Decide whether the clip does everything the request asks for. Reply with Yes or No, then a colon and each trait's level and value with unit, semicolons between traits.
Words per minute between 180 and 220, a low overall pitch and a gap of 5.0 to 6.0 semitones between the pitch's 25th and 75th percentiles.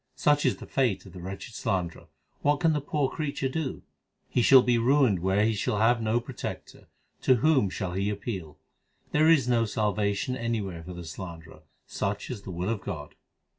Yes: average, 190 wpm; low, 110 Hz; wide, 5.6 semitones